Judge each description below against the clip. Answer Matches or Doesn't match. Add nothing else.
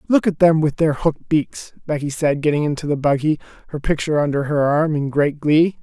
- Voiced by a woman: Doesn't match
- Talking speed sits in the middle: Doesn't match